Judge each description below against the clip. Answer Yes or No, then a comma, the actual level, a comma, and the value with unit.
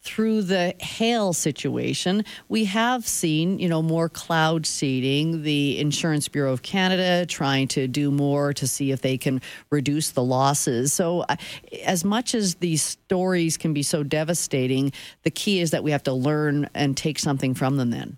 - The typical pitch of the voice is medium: Yes, medium, 155 Hz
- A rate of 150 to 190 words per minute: Yes, average, 175 wpm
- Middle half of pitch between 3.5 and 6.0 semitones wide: Yes, average, 4.2 semitones